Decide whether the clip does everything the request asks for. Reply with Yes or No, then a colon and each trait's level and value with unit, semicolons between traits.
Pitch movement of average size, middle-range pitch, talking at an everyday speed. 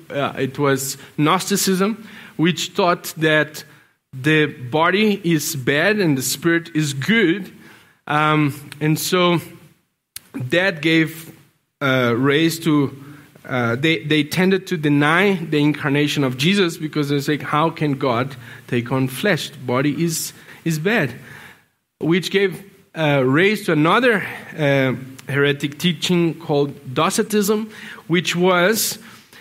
No: average, 3.8 semitones; medium, 155 Hz; slow, 120 wpm